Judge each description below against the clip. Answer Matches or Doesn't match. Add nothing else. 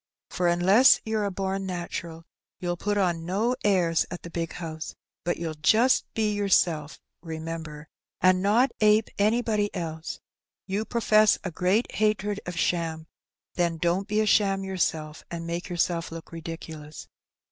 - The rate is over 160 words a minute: Doesn't match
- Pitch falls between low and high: Matches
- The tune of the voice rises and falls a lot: Doesn't match